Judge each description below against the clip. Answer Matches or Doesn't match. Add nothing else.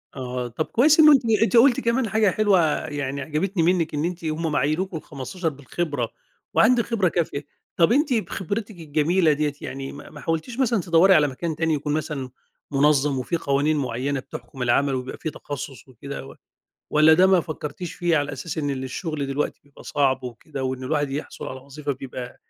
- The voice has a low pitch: Doesn't match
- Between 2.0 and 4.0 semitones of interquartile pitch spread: Doesn't match